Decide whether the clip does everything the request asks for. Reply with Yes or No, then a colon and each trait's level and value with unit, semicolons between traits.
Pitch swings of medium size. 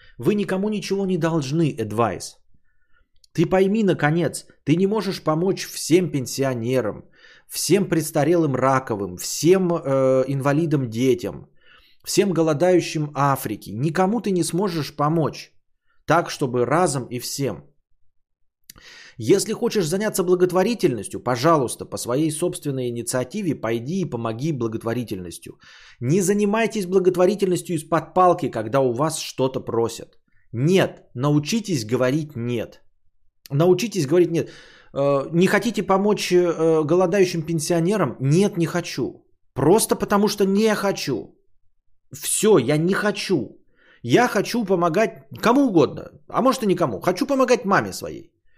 No: wide, 6.4 semitones